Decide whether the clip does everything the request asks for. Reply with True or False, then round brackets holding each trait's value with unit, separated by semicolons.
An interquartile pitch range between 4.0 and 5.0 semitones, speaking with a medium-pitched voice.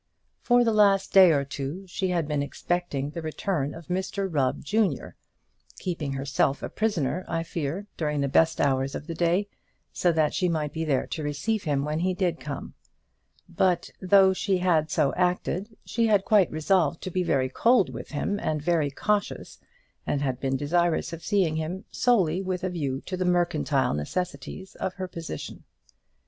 True (4.3 semitones; 170 Hz)